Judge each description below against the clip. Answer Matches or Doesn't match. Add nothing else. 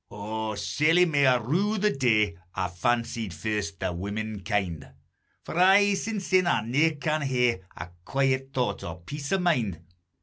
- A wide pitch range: Matches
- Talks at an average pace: Matches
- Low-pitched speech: Matches